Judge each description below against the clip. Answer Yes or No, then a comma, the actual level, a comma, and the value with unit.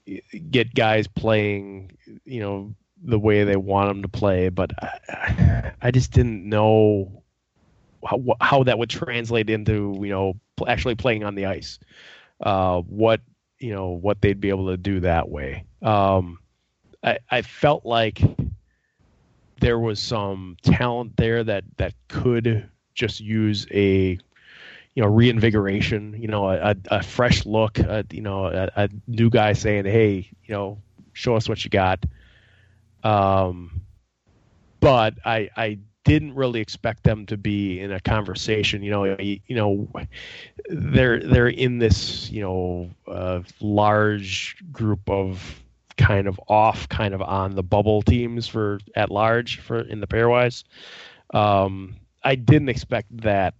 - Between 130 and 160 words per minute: Yes, average, 150 wpm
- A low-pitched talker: Yes, low, 105 Hz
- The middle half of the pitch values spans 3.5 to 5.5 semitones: No, average, 2.9 semitones